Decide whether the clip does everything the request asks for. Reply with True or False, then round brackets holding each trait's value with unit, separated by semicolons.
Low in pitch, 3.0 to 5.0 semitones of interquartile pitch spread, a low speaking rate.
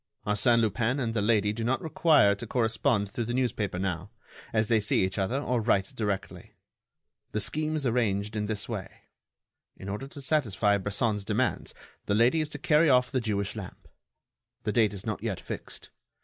False (110 Hz; 3.7 semitones; 185 wpm)